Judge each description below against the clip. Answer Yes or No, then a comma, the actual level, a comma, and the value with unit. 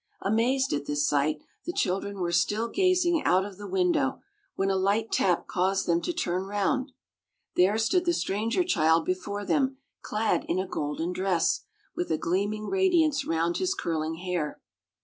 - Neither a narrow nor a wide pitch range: No, wide, 7.5 semitones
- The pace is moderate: Yes, average, 170 wpm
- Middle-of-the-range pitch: No, high, 195 Hz